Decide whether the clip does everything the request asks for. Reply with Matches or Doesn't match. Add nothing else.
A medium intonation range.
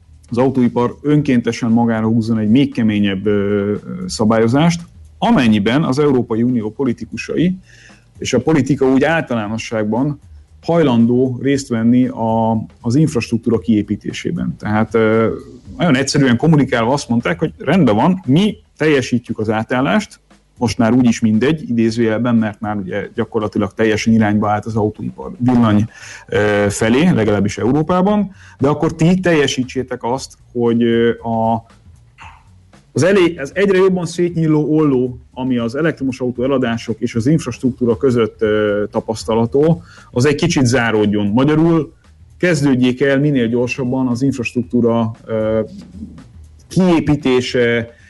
Matches